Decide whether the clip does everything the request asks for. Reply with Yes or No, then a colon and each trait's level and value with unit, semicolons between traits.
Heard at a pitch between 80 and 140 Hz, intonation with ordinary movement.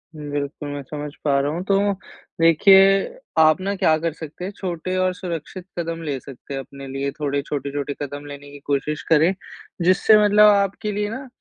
No: medium, 155 Hz; average, 4.6 semitones